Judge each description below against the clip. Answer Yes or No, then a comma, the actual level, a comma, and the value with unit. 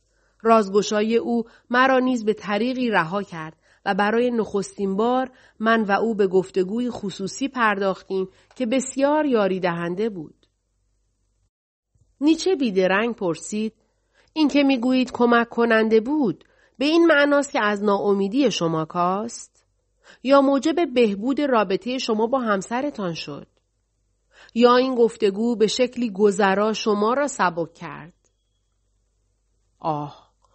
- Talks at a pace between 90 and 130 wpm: Yes, average, 120 wpm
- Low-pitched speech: No, high, 210 Hz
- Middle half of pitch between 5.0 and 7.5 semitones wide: Yes, wide, 5.5 semitones